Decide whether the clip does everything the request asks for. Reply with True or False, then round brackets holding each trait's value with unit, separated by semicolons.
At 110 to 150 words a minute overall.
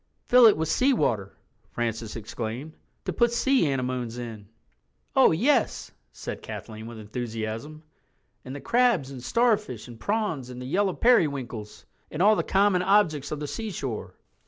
True (145 wpm)